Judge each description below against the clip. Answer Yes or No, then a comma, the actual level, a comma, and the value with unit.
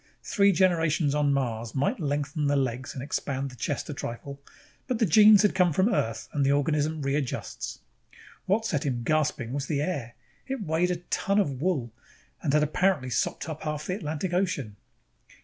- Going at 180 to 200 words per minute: Yes, average, 185 wpm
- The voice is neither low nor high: Yes, medium, 150 Hz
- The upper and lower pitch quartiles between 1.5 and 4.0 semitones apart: No, average, 4.7 semitones